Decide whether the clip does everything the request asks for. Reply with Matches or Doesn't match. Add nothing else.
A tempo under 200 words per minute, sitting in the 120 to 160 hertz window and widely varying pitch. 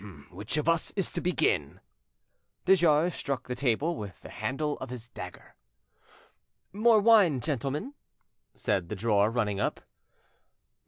Matches